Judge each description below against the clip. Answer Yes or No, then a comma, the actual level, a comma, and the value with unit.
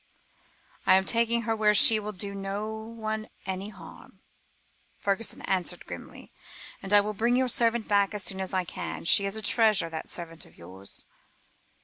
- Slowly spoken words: No, average, 175 wpm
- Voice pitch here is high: Yes, high, 205 Hz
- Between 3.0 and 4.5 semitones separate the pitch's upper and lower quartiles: No, narrow, 2.4 semitones